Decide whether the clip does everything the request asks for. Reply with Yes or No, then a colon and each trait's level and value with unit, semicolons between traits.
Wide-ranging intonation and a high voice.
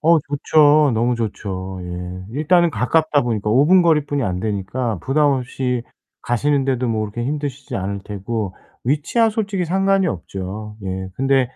No: wide, 6.3 semitones; low, 125 Hz